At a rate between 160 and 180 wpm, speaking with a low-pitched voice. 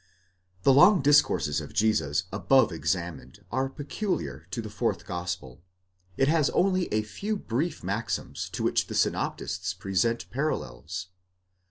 No: slow, 135 wpm; low, 110 Hz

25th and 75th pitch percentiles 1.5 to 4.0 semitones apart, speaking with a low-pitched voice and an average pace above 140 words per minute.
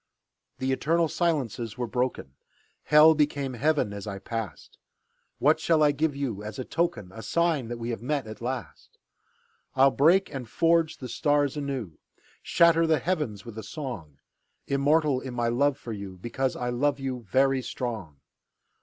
No: average, 4.6 semitones; low, 130 Hz; average, 165 wpm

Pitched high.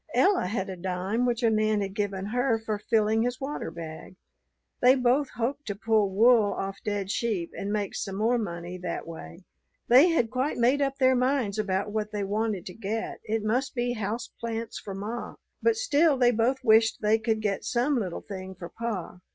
Yes: high, 220 Hz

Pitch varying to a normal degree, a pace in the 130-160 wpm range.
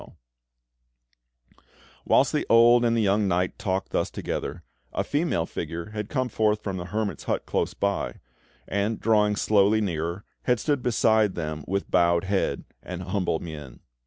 Yes: average, 3.8 semitones; average, 155 wpm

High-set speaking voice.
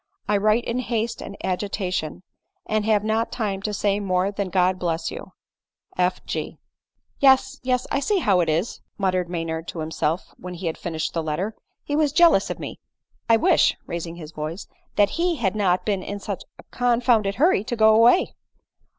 Yes: high, 200 Hz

